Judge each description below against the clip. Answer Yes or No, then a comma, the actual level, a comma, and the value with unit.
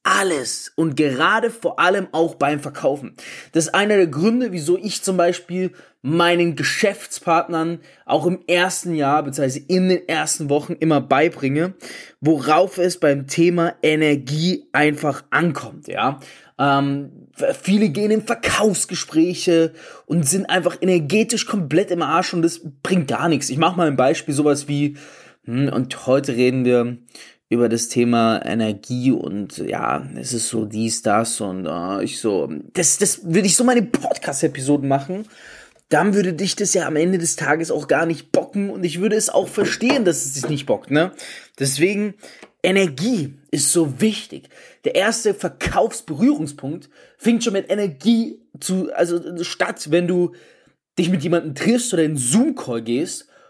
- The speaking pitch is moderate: Yes, medium, 170 Hz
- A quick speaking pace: No, average, 155 wpm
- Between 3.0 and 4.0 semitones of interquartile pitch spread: No, average, 4.6 semitones